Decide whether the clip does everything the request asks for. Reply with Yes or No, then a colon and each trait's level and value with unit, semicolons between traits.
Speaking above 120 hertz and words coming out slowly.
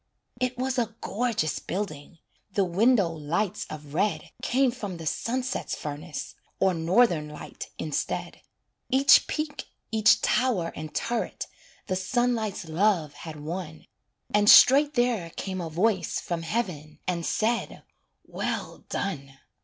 Yes: high, 190 Hz; slow, 130 wpm